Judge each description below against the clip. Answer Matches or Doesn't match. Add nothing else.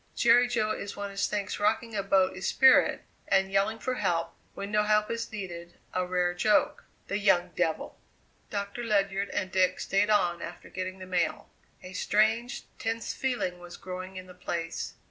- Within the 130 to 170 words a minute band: Doesn't match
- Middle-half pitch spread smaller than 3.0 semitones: Matches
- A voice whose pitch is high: Matches